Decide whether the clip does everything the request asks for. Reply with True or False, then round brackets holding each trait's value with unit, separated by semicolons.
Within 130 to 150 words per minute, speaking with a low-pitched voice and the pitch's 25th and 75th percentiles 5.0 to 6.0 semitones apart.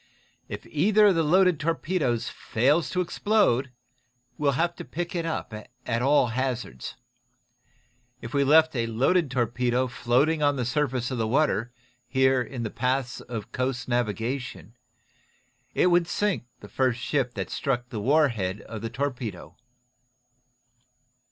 False (145 wpm; 130 Hz; 4.4 semitones)